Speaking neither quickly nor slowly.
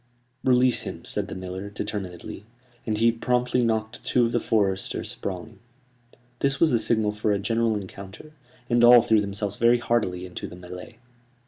Yes: average, 165 wpm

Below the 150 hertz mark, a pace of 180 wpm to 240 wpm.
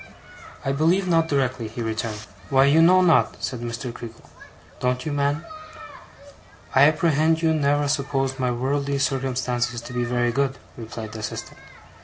No: low, 135 Hz; average, 155 wpm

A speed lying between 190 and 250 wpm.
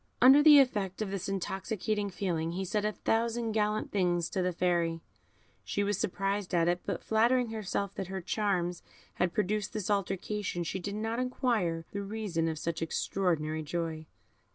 No: average, 170 wpm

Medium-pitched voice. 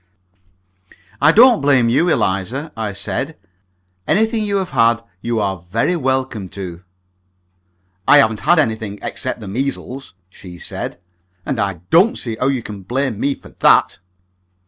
No: low, 120 Hz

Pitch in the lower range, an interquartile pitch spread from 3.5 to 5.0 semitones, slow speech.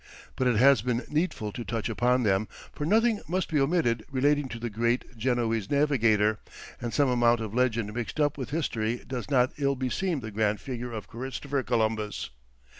No: low, 120 Hz; average, 3.8 semitones; average, 185 wpm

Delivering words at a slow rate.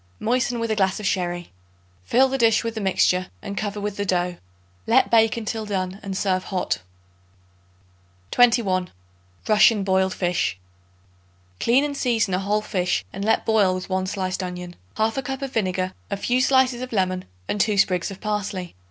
No: average, 175 wpm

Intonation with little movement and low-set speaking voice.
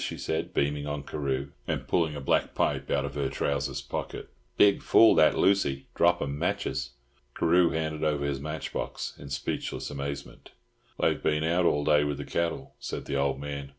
Yes: narrow, 2.2 semitones; very low, 75 Hz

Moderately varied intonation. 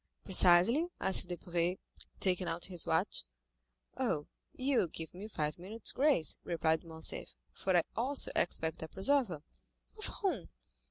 No: wide, 6.0 semitones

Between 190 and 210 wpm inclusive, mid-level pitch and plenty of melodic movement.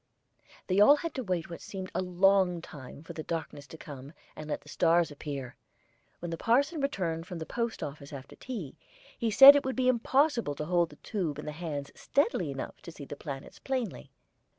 Yes: fast, 205 wpm; medium, 175 Hz; wide, 7.6 semitones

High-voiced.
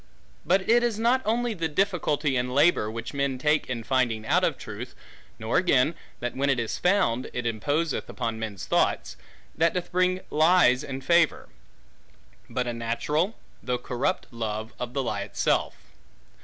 No: low, 135 Hz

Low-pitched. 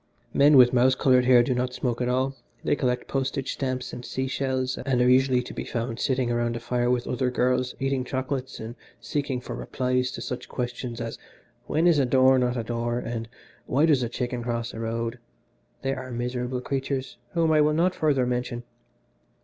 Yes: low, 125 Hz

